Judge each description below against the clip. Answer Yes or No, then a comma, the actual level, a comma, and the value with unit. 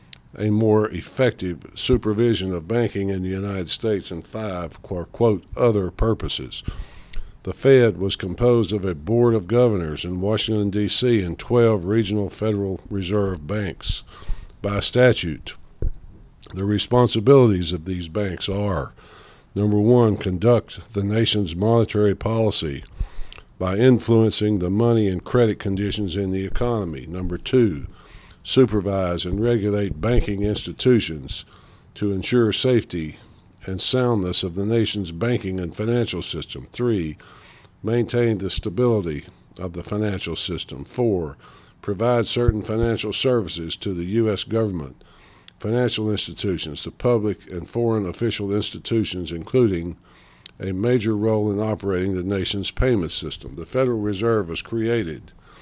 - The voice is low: Yes, low, 105 Hz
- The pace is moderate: No, slow, 125 wpm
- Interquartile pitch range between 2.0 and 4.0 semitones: Yes, average, 3.6 semitones